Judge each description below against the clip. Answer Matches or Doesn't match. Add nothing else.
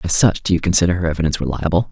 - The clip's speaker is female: Doesn't match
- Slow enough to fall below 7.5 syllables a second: Doesn't match